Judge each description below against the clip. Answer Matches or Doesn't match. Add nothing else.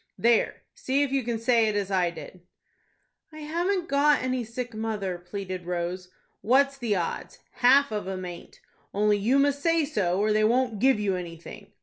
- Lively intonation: Matches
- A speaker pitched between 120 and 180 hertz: Doesn't match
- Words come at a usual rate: Matches